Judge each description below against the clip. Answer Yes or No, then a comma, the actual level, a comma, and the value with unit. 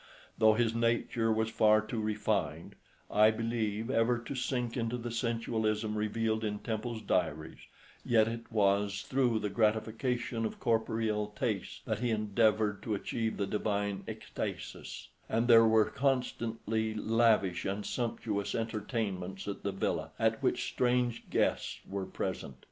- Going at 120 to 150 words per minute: Yes, average, 140 wpm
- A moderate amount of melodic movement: No, narrow, 1.7 semitones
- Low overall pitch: Yes, low, 110 Hz